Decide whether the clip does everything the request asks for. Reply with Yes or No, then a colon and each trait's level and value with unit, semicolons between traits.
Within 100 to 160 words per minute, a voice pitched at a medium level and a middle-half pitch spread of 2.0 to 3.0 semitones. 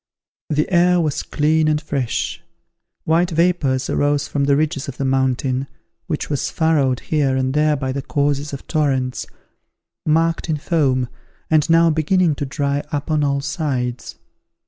Yes: average, 155 wpm; medium, 145 Hz; narrow, 2.6 semitones